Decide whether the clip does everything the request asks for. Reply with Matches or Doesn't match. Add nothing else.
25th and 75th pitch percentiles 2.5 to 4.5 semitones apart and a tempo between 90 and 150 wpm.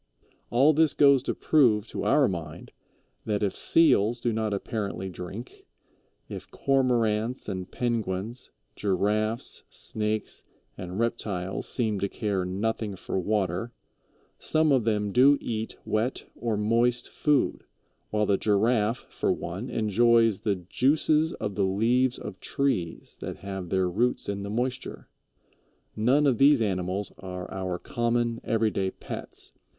Matches